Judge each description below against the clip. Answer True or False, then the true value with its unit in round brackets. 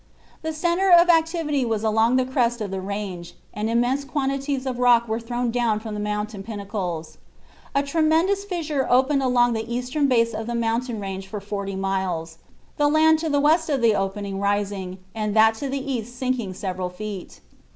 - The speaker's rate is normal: True (185 wpm)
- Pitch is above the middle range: True (235 Hz)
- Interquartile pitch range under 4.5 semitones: False (5.2 semitones)